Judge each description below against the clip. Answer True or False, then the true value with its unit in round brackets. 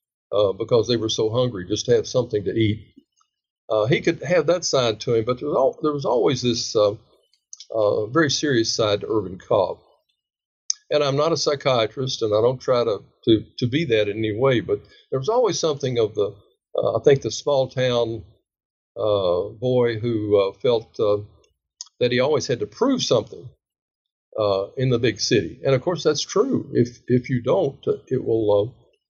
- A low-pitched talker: True (125 Hz)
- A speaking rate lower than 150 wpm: False (200 wpm)